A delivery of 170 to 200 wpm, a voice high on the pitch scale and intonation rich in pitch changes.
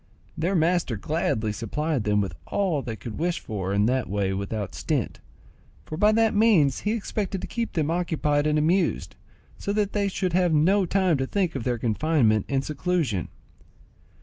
No: average, 175 wpm; medium, 155 Hz; wide, 8.4 semitones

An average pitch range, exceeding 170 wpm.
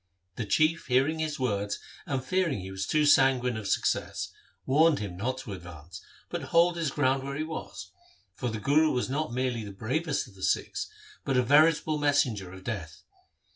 No: wide, 6.7 semitones; average, 185 wpm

